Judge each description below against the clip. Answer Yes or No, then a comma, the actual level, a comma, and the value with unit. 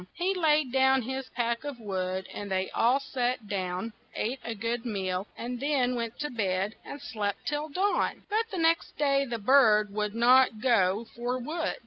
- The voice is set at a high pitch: Yes, high, 240 Hz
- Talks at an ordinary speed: Yes, average, 180 wpm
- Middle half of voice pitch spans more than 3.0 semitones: Yes, average, 4.7 semitones